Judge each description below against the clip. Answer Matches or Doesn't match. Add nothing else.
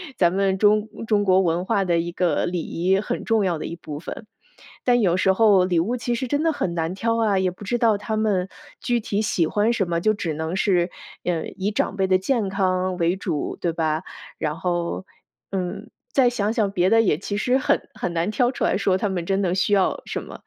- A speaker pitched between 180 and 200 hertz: Matches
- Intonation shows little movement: Doesn't match